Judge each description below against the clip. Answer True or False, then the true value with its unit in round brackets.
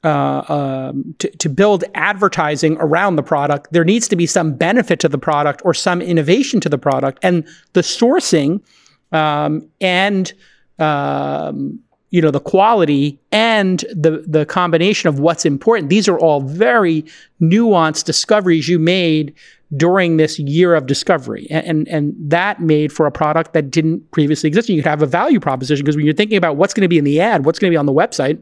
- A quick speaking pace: False (195 wpm)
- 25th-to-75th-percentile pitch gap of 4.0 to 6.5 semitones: False (3.3 semitones)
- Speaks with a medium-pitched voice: True (165 Hz)